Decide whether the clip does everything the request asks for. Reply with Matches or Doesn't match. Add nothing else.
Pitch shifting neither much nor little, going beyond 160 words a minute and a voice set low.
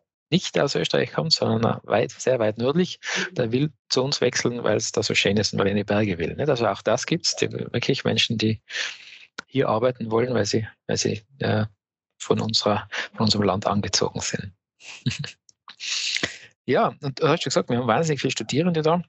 Matches